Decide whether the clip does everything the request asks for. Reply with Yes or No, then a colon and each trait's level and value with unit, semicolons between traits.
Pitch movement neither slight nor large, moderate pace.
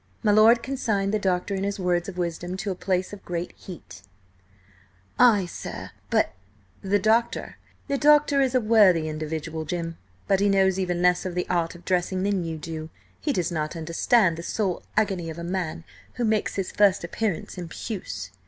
Yes: average, 3.3 semitones; average, 180 wpm